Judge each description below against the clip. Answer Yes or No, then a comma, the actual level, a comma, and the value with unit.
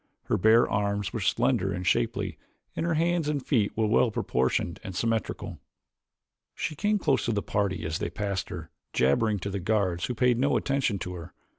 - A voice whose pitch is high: No, low, 105 Hz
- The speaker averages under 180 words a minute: No, average, 185 wpm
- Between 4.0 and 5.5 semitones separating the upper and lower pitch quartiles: Yes, average, 4.9 semitones